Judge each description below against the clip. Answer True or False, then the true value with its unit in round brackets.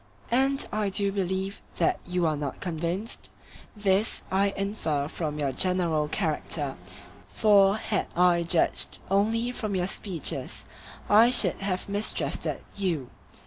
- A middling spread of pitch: True (3.6 semitones)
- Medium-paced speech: False (125 wpm)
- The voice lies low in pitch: False (190 Hz)